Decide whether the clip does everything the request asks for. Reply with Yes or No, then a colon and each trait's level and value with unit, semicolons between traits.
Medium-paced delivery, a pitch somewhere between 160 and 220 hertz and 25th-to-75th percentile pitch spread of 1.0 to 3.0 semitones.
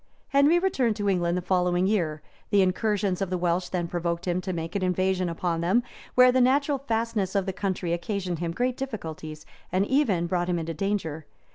No: average, 195 wpm; medium, 185 Hz; average, 3.9 semitones